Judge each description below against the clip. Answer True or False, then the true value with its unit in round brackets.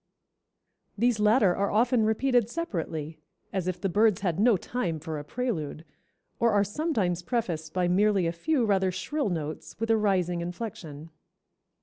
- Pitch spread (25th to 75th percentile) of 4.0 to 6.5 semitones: True (4.9 semitones)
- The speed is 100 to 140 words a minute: False (155 wpm)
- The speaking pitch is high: True (195 Hz)